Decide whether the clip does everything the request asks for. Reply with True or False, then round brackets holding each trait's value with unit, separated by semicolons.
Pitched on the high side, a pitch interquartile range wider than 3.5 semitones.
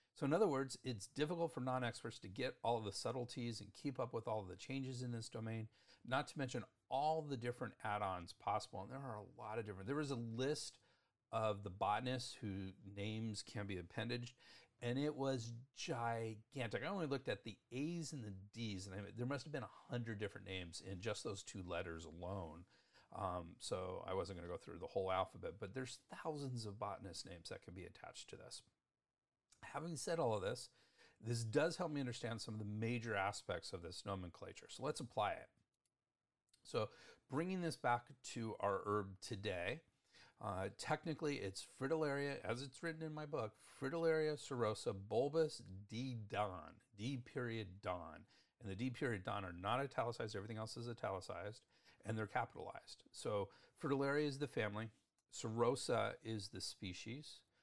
False (120 Hz; 4.8 semitones)